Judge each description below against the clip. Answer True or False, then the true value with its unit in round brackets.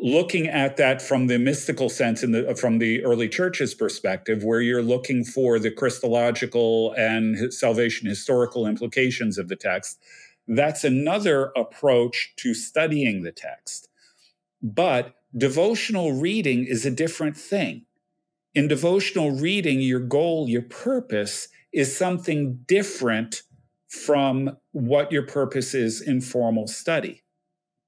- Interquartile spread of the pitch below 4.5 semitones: True (4.1 semitones)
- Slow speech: True (125 wpm)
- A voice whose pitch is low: True (130 Hz)